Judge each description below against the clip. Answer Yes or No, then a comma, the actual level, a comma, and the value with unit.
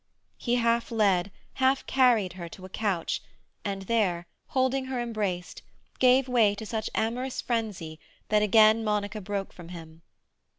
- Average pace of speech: Yes, average, 145 wpm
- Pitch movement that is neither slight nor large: Yes, average, 4.0 semitones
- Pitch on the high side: Yes, high, 215 Hz